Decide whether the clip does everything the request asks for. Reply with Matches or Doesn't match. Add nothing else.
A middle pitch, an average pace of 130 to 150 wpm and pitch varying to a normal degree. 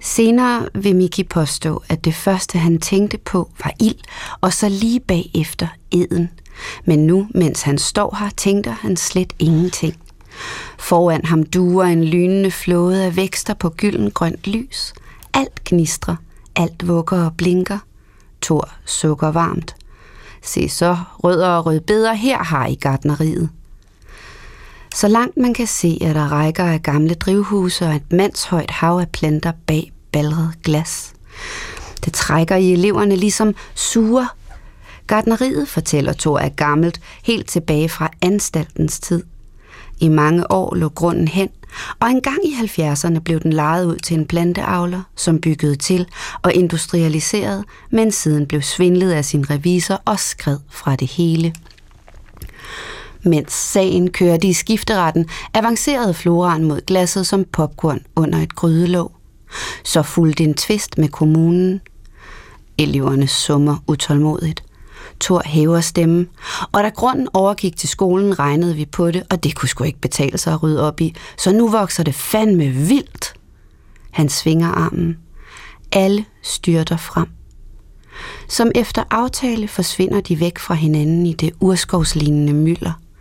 Matches